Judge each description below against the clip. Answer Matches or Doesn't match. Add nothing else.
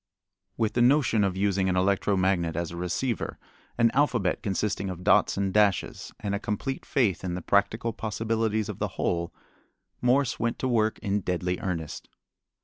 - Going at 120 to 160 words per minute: Doesn't match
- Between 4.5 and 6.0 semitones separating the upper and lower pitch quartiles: Doesn't match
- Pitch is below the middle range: Matches